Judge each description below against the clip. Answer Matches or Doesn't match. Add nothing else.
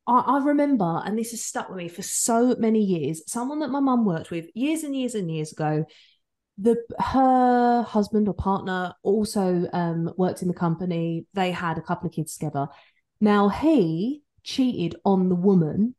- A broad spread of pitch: Matches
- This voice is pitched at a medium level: Doesn't match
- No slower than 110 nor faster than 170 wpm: Doesn't match